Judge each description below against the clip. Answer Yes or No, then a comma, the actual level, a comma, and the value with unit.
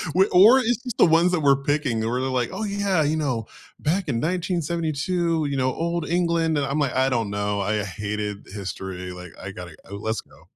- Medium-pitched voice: Yes, medium, 145 Hz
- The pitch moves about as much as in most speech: No, wide, 8.2 semitones